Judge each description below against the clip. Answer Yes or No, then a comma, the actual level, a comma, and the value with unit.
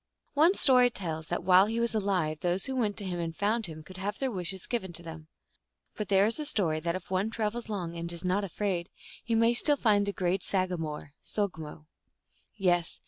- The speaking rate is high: Yes, fast, 210 wpm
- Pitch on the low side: No, high, 190 Hz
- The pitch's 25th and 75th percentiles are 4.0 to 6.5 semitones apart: Yes, average, 4.3 semitones